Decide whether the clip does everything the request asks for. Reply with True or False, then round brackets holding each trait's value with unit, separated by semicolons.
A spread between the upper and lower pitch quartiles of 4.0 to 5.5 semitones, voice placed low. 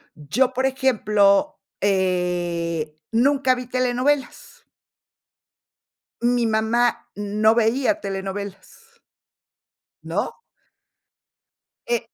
False (4.7 semitones; 225 Hz)